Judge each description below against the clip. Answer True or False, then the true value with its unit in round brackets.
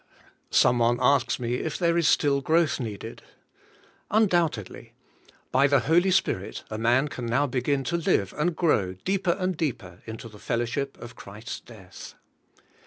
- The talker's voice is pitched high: False (135 Hz)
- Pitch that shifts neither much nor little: False (6.1 semitones)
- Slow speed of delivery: False (155 wpm)